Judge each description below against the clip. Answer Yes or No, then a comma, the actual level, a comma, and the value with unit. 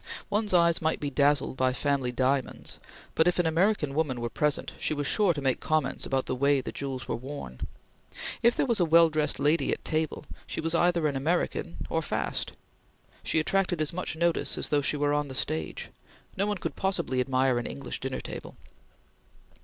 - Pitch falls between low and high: Yes, medium, 150 Hz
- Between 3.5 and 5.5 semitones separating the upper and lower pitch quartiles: Yes, average, 4.0 semitones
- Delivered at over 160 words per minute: Yes, average, 200 wpm